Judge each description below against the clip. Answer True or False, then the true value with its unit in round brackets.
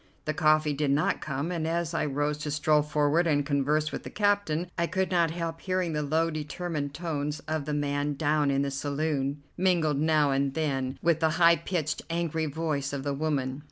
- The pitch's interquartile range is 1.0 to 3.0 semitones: True (2.4 semitones)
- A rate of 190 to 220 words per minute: True (200 wpm)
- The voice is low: False (155 Hz)